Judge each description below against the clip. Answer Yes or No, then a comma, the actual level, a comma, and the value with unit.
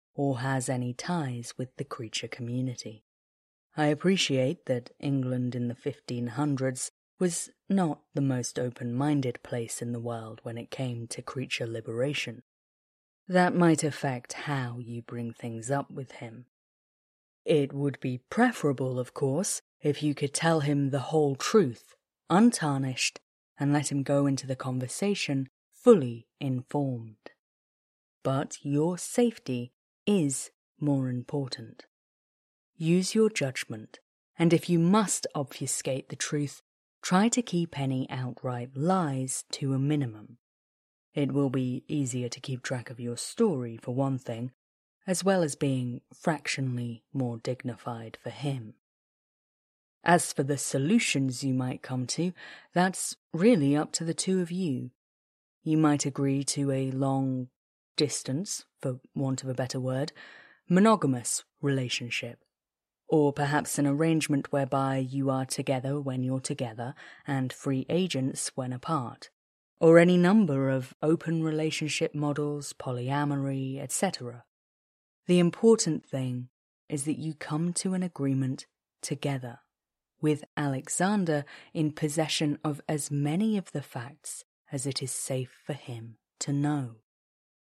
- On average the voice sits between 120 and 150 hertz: Yes, medium, 140 Hz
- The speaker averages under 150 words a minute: Yes, slow, 135 wpm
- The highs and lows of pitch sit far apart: No, average, 3.3 semitones